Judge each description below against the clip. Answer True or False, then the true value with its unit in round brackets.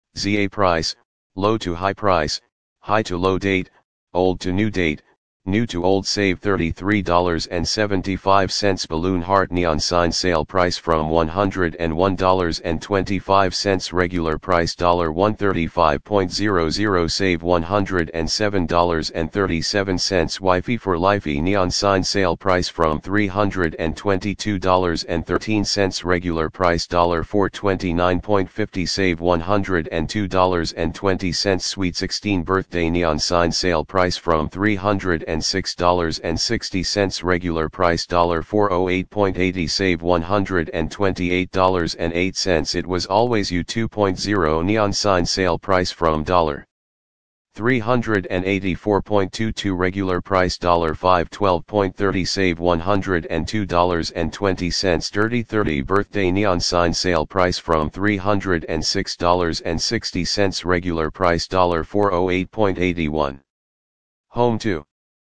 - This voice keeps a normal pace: False (85 wpm)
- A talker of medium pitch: False (90 Hz)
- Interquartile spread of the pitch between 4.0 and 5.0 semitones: False (2.6 semitones)